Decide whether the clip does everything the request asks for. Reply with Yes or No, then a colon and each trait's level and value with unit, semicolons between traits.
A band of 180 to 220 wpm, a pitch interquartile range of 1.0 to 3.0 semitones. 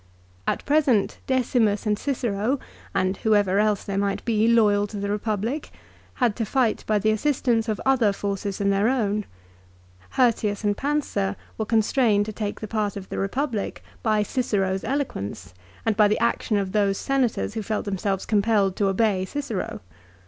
No: average, 170 wpm; narrow, 2.6 semitones